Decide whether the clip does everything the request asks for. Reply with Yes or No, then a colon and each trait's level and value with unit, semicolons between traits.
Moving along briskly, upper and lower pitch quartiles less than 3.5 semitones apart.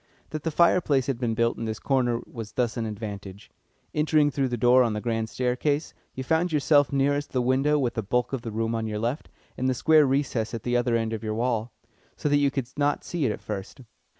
No: fast, 235 wpm; average, 4.0 semitones